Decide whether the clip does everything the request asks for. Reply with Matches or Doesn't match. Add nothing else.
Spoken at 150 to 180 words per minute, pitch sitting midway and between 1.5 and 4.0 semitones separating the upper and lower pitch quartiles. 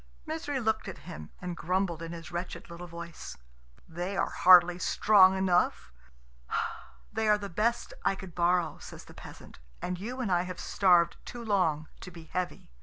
Matches